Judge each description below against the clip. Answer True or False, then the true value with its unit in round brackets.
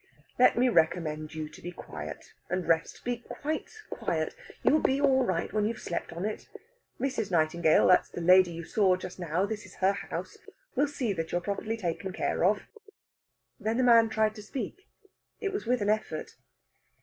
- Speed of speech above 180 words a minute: True (195 wpm)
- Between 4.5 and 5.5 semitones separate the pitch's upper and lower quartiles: True (5.2 semitones)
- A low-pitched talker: False (200 Hz)